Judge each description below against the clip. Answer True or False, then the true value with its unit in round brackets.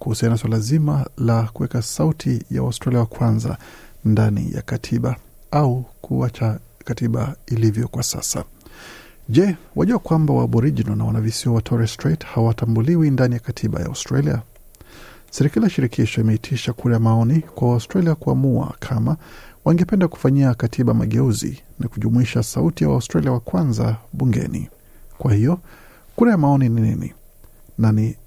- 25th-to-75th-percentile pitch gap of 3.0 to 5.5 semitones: True (3.6 semitones)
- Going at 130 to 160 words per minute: True (140 wpm)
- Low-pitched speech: True (120 Hz)